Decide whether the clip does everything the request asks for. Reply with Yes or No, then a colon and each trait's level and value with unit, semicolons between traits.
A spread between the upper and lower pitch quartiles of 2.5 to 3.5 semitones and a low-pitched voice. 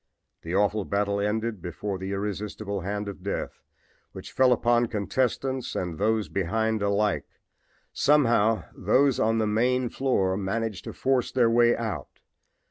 Yes: average, 2.9 semitones; low, 105 Hz